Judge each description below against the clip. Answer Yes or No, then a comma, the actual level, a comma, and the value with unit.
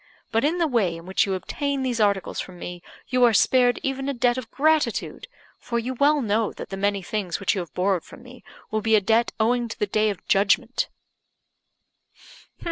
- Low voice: No, high, 225 Hz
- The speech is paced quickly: Yes, fast, 210 wpm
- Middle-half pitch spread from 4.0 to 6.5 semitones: Yes, average, 4.4 semitones